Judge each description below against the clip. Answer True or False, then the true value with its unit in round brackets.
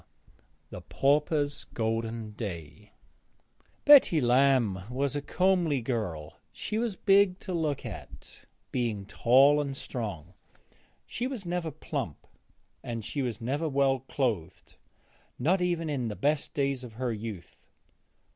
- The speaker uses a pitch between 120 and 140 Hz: True (135 Hz)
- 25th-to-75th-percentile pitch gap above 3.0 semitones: True (5.6 semitones)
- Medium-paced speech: False (125 wpm)